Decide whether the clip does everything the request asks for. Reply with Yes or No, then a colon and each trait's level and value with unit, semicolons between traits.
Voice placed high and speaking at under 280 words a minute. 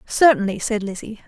Yes: high, 215 Hz; average, 140 wpm